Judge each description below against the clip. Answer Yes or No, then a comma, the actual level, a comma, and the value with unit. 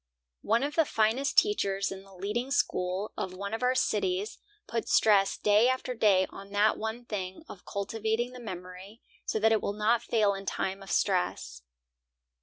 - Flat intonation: No, average, 3.2 semitones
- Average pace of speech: Yes, average, 180 wpm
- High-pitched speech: Yes, high, 210 Hz